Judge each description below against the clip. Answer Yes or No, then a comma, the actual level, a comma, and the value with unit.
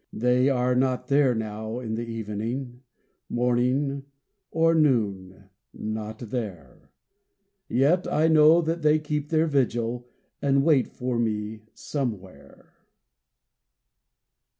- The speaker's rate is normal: No, slow, 105 wpm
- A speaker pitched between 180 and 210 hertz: No, low, 125 Hz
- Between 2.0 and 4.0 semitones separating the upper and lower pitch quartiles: No, average, 4.4 semitones